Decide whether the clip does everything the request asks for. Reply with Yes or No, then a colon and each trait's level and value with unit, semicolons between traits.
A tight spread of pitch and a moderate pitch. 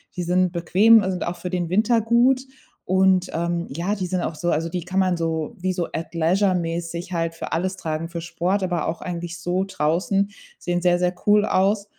Yes: narrow, 2.0 semitones; medium, 180 Hz